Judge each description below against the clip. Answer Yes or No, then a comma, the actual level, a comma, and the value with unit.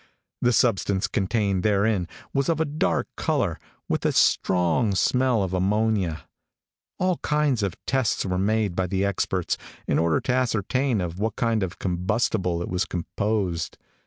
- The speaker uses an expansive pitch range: No, average, 4.2 semitones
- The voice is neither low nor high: No, low, 100 Hz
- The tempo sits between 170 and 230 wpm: No, average, 155 wpm